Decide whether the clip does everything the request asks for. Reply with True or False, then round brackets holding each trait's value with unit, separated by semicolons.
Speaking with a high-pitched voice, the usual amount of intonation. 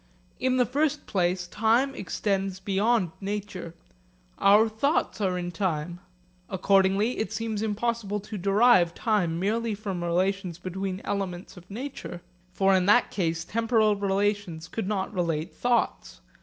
True (195 Hz; 3.4 semitones)